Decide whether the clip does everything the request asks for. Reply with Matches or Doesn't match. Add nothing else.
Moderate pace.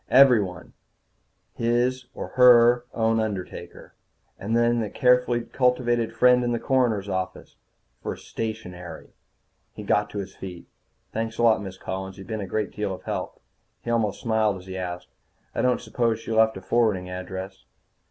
Matches